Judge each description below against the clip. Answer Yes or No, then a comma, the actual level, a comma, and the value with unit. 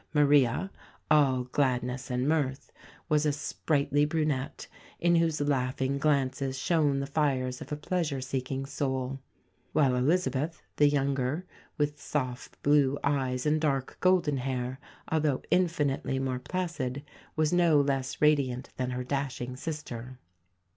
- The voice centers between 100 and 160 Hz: Yes, medium, 140 Hz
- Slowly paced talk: Yes, slow, 130 wpm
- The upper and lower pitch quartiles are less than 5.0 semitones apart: Yes, narrow, 2.6 semitones